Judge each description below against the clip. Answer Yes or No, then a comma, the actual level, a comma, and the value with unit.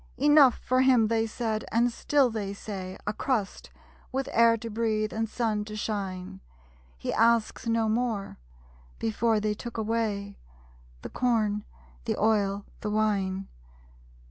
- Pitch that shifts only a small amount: Yes, narrow, 2.0 semitones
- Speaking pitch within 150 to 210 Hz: No, high, 220 Hz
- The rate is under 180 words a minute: Yes, average, 140 wpm